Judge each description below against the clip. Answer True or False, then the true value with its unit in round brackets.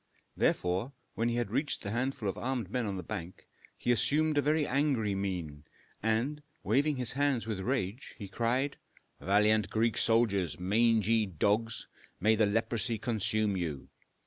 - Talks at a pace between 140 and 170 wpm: True (150 wpm)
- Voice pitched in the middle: False (110 Hz)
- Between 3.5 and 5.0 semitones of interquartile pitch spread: True (3.9 semitones)